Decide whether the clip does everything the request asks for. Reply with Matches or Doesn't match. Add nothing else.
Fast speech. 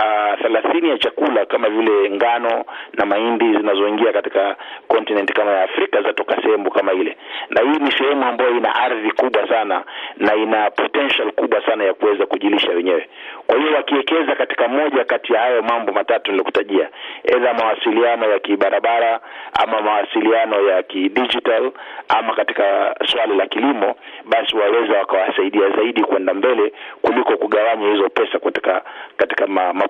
Matches